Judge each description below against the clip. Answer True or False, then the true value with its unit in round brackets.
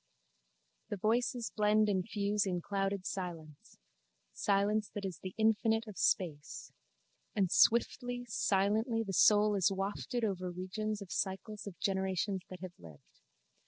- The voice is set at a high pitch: True (200 Hz)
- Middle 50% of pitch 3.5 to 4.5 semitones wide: False (2.4 semitones)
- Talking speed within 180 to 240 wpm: False (135 wpm)